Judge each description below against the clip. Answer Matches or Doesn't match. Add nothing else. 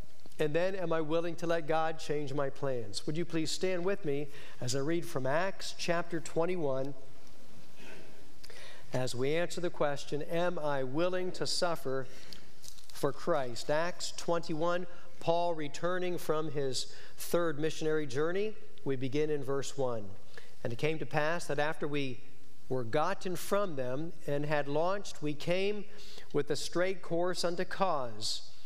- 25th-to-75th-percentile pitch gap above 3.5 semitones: Matches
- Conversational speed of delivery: Matches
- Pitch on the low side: Doesn't match